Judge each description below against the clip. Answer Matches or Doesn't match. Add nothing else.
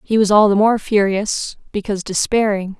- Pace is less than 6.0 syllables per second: Matches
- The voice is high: Matches